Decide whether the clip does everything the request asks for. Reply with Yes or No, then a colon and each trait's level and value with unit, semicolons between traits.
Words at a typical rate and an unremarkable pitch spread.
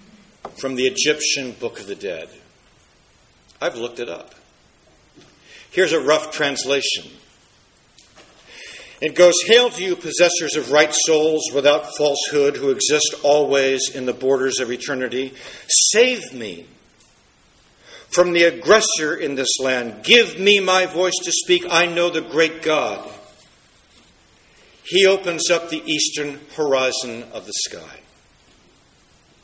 No: slow, 125 wpm; average, 4.7 semitones